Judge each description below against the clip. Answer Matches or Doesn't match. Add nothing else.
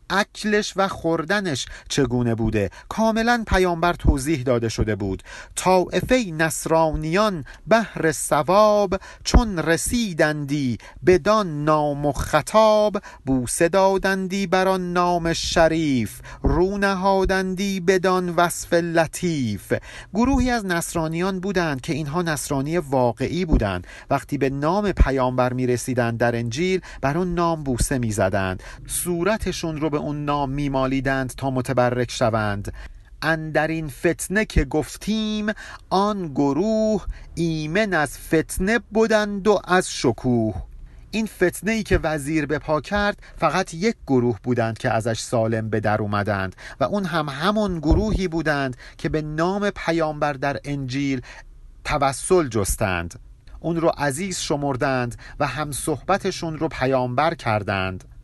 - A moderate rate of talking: Matches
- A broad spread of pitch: Matches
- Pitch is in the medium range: Matches